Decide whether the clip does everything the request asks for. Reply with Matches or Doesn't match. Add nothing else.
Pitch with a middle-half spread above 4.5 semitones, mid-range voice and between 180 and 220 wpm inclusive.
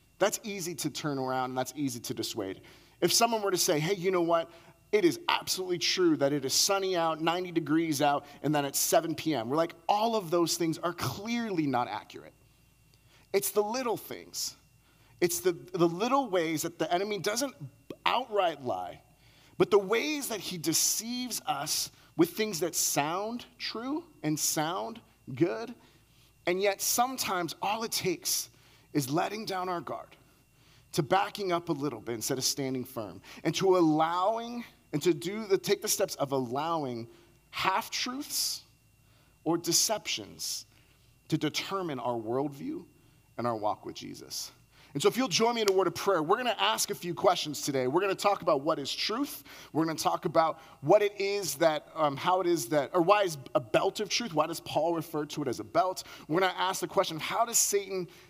Matches